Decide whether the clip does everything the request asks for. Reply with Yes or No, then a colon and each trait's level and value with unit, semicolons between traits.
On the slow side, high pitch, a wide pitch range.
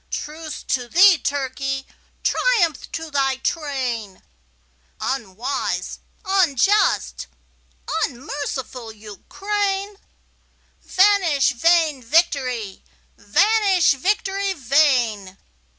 Yes: slow, 70 wpm; very high, 285 Hz; wide, 6.9 semitones